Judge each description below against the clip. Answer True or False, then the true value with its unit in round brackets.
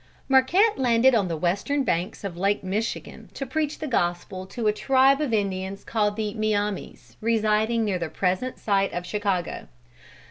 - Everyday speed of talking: True (165 wpm)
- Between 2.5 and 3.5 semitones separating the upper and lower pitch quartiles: False (4.7 semitones)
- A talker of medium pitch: False (210 Hz)